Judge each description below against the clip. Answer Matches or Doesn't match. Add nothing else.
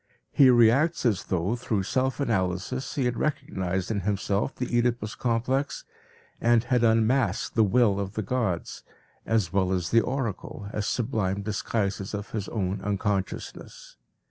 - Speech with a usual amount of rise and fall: Matches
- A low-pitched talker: Matches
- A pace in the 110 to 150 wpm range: Matches